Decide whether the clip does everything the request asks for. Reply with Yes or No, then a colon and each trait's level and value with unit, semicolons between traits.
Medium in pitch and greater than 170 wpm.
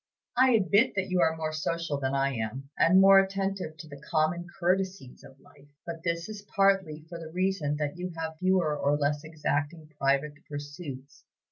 Yes: medium, 160 Hz; average, 180 wpm